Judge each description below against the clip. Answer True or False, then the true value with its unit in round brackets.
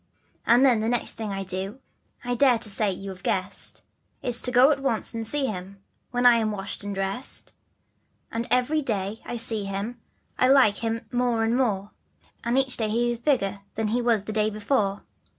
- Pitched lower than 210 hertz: False (225 Hz)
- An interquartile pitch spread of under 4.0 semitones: True (3.3 semitones)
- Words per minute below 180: False (205 wpm)